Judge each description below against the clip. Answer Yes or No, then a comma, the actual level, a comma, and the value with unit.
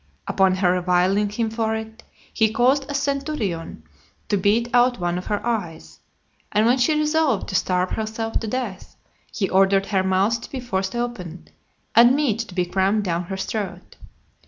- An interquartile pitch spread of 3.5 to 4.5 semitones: Yes, average, 4.2 semitones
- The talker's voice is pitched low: No, high, 215 Hz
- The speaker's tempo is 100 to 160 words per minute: No, average, 175 wpm